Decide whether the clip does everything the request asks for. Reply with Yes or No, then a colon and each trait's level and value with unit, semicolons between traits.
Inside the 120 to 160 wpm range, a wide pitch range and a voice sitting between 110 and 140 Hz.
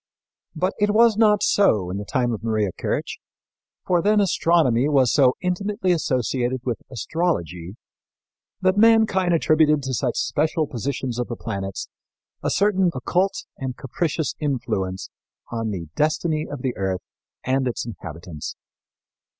Yes: average, 140 wpm; wide, 7.6 semitones; low, 135 Hz